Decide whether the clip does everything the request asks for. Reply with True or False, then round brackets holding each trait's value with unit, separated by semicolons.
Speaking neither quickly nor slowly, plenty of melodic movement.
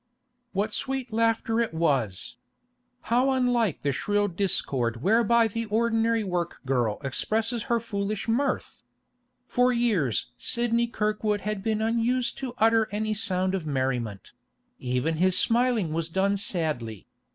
False (130 wpm; 6.0 semitones)